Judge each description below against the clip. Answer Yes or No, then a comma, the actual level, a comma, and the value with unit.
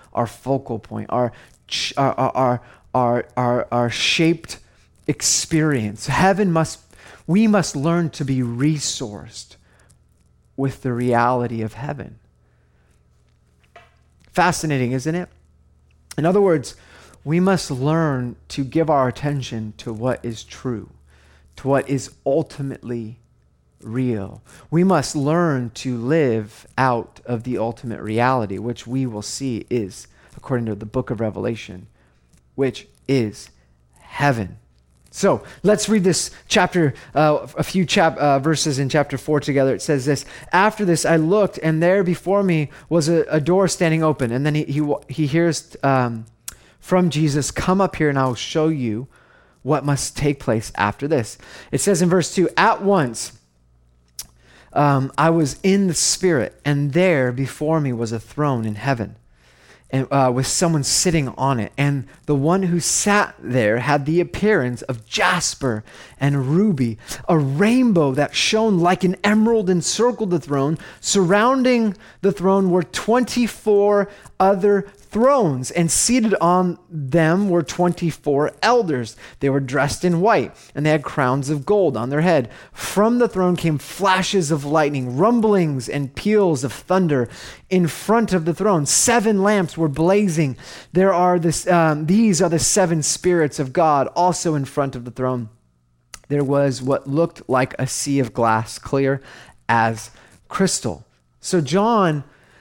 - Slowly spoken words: No, average, 150 wpm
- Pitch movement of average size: No, wide, 6.4 semitones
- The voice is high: No, medium, 145 Hz